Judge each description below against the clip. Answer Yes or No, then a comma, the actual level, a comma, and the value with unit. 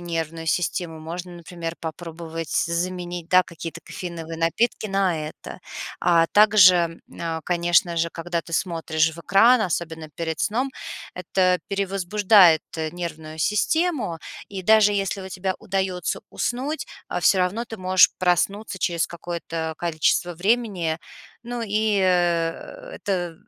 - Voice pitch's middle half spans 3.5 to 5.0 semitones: No, average, 3.0 semitones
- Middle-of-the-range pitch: Yes, medium, 175 Hz